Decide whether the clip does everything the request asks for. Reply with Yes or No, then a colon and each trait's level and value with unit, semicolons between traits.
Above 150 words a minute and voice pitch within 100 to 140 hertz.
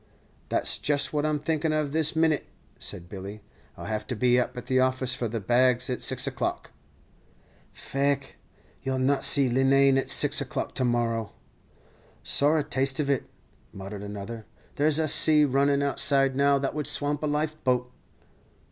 Yes: average, 175 wpm; low, 135 Hz